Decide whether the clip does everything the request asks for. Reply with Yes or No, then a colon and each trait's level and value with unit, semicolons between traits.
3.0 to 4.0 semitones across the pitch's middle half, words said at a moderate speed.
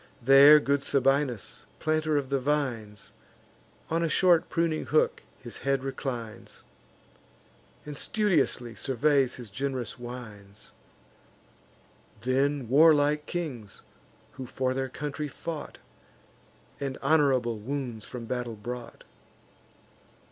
No: average, 3.4 semitones; slow, 105 wpm